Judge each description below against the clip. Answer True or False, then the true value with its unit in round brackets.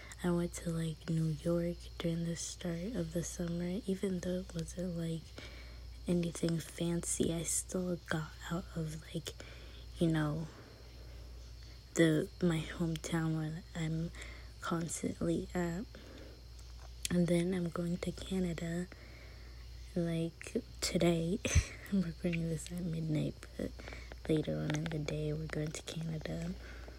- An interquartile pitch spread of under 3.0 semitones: True (2.6 semitones)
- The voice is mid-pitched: True (165 Hz)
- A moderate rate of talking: False (125 wpm)